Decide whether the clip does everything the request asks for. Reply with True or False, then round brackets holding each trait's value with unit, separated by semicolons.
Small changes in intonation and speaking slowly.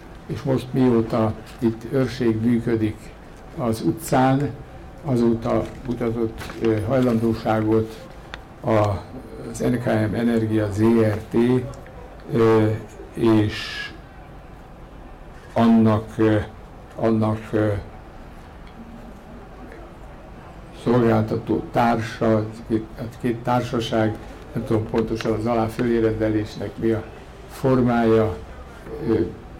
True (1.3 semitones; 60 wpm)